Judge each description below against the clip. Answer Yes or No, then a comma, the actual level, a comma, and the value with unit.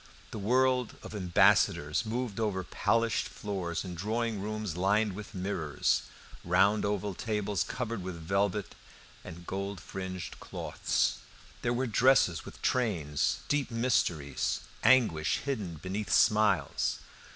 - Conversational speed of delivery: No, slow, 120 wpm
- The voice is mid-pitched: No, low, 100 Hz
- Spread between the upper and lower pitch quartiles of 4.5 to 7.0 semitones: No, average, 3.7 semitones